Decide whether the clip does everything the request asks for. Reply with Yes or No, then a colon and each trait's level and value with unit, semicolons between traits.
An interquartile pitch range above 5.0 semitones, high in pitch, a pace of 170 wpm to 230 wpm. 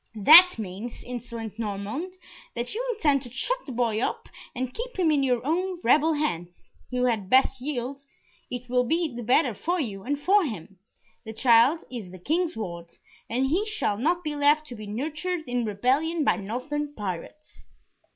Yes: wide, 5.6 semitones; very high, 255 Hz; average, 180 wpm